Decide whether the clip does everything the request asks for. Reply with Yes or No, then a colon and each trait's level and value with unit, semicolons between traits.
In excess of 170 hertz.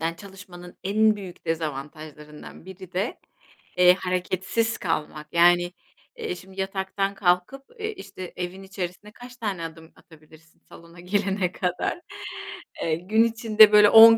Yes: medium, 185 Hz